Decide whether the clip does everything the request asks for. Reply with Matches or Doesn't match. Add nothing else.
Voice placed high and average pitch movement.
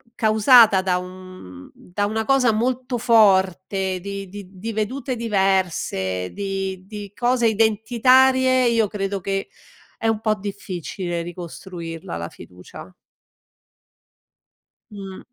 Matches